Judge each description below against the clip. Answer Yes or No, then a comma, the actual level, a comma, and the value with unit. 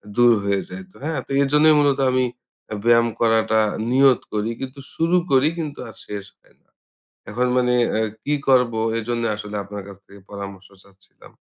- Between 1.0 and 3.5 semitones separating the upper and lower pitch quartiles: No, average, 4.7 semitones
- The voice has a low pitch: Yes, low, 120 Hz